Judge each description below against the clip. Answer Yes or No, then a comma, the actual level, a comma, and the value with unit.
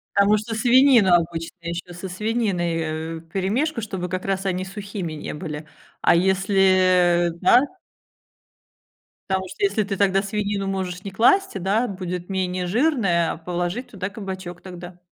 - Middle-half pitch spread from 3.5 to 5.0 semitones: No, narrow, 2.6 semitones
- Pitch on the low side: No, high, 190 Hz